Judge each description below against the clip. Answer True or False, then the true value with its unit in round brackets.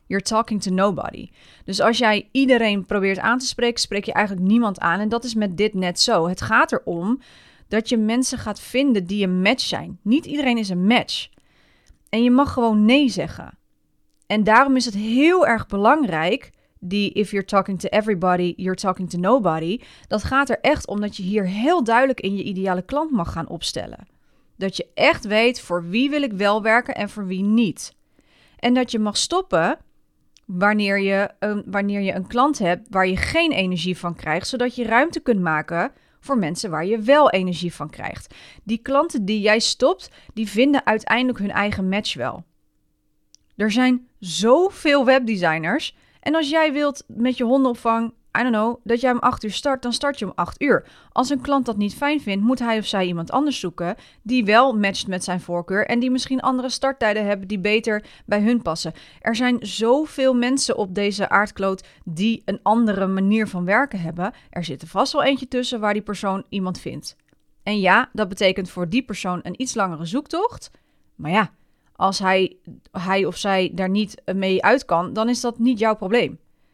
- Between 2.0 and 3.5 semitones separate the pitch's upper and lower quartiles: False (4.5 semitones)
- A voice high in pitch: True (215 Hz)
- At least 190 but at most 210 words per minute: True (195 wpm)